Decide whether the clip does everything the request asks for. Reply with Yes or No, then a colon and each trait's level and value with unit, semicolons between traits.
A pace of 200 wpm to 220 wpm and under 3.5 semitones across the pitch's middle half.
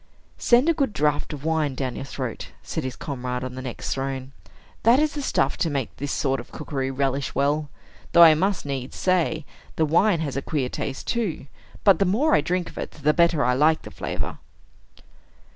No: fast, 205 wpm; average, 4.2 semitones